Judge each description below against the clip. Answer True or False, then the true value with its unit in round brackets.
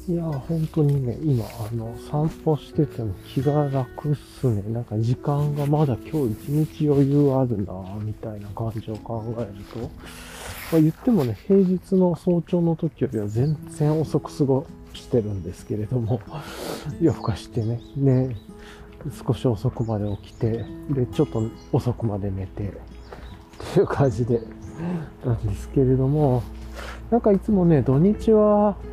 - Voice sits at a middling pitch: False (125 Hz)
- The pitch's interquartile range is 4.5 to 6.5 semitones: True (5.9 semitones)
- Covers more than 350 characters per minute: False (280 characters per minute)